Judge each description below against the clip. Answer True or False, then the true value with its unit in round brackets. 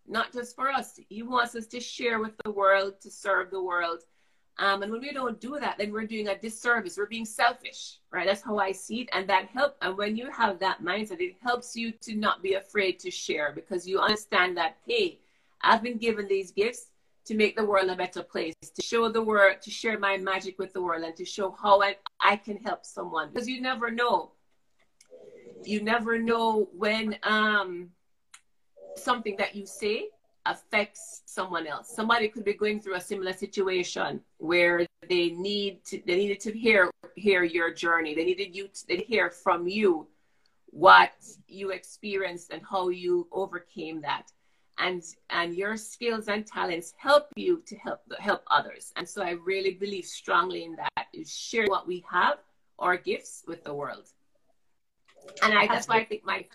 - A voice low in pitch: False (205 Hz)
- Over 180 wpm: True (195 wpm)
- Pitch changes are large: False (3.6 semitones)